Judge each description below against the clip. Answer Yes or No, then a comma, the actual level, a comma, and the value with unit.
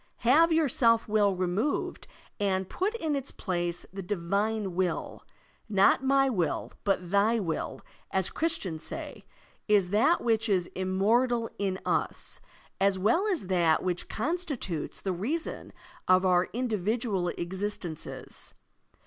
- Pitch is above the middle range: Yes, high, 200 Hz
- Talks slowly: Yes, slow, 130 wpm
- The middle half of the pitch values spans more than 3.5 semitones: Yes, average, 4.6 semitones